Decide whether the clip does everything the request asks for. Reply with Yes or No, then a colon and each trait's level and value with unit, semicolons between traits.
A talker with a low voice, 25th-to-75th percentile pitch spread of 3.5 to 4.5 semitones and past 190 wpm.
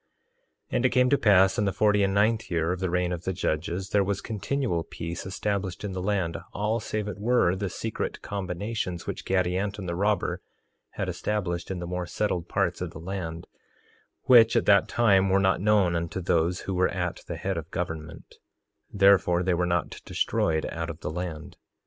No: very low, 95 Hz; average, 2.8 semitones; average, 200 wpm